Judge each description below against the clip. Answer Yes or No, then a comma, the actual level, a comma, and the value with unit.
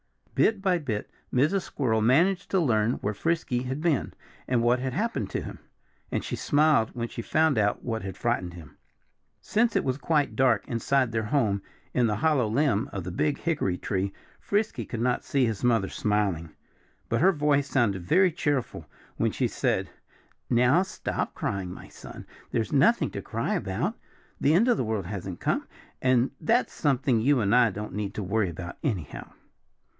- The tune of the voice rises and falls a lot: Yes, wide, 5.9 semitones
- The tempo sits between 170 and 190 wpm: Yes, average, 180 wpm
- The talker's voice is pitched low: Yes, low, 120 Hz